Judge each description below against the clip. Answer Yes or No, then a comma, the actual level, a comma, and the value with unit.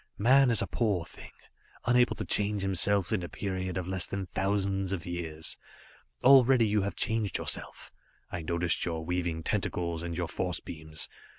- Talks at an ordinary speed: Yes, average, 170 wpm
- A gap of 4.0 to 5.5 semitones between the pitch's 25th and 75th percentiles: No, average, 3.2 semitones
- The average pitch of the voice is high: No, very low, 95 Hz